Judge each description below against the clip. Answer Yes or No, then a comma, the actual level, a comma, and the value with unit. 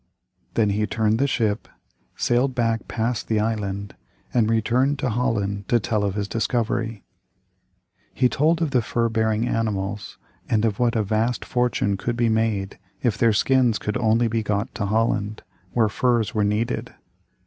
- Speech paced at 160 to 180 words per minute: Yes, average, 165 wpm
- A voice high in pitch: No, low, 110 Hz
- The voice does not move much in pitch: Yes, narrow, 2.2 semitones